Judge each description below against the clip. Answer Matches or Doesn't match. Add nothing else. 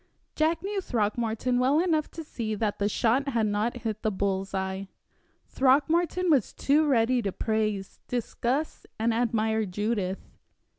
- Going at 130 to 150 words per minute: Matches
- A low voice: Doesn't match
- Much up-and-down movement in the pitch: Doesn't match